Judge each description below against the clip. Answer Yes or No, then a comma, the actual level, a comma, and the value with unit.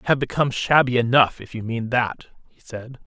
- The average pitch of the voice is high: No, low, 120 Hz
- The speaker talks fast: Yes, fast, 210 wpm